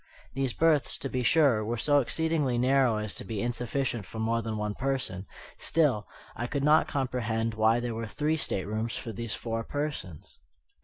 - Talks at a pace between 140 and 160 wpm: No, average, 175 wpm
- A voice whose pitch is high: No, low, 120 Hz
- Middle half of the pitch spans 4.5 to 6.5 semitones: No, average, 3.7 semitones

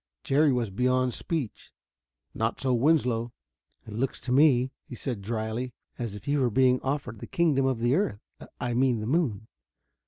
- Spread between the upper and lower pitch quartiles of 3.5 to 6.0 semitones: No, average, 2.8 semitones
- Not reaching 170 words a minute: No, average, 175 wpm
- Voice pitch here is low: Yes, low, 125 Hz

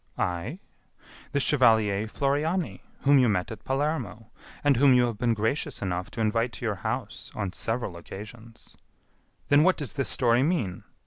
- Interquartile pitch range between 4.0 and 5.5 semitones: Yes, average, 4.6 semitones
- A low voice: Yes, low, 115 Hz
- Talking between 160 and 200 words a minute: Yes, average, 165 wpm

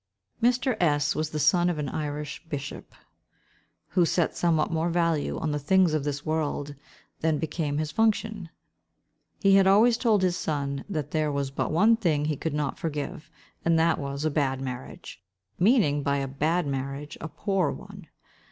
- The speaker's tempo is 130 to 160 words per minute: No, average, 170 wpm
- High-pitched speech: No, medium, 155 Hz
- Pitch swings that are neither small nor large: Yes, average, 3.5 semitones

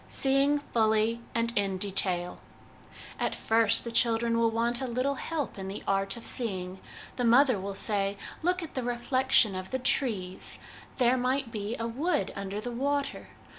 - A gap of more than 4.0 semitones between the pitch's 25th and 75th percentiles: Yes, average, 4.4 semitones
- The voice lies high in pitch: Yes, high, 230 Hz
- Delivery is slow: No, average, 170 wpm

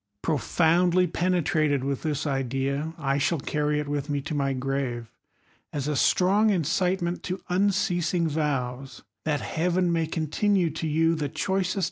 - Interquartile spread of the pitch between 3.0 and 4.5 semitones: Yes, average, 3.9 semitones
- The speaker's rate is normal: Yes, average, 165 wpm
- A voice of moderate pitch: Yes, medium, 155 Hz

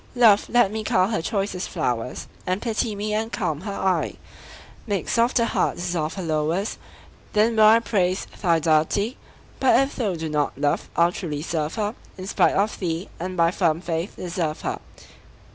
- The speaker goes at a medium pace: Yes, average, 180 wpm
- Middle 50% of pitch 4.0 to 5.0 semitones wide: Yes, average, 4.6 semitones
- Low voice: No, medium, 185 Hz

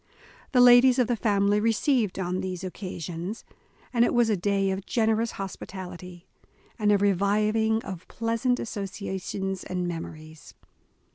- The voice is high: Yes, high, 200 Hz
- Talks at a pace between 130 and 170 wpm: Yes, average, 140 wpm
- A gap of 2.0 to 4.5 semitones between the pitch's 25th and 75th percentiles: Yes, average, 3.4 semitones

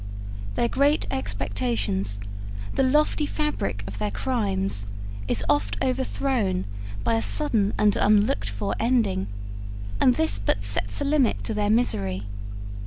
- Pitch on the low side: No, medium, 180 Hz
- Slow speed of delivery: Yes, slow, 130 wpm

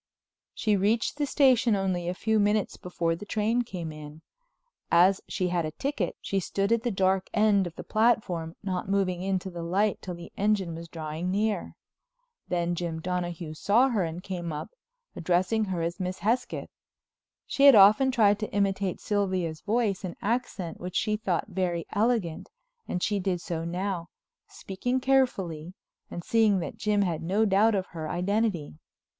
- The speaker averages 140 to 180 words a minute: Yes, average, 170 wpm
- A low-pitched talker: No, high, 190 Hz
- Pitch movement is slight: No, average, 3.6 semitones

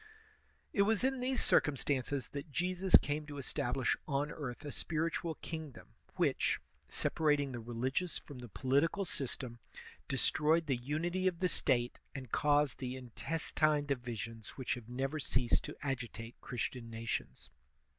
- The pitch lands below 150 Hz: Yes, medium, 140 Hz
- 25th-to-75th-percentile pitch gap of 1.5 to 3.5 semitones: No, average, 4.2 semitones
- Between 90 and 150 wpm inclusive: Yes, average, 145 wpm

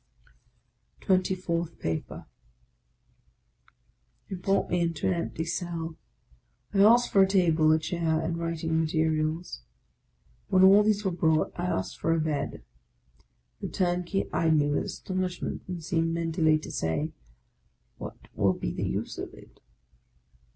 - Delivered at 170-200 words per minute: No, average, 145 wpm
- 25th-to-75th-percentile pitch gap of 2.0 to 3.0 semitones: Yes, narrow, 2.6 semitones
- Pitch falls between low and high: Yes, medium, 170 Hz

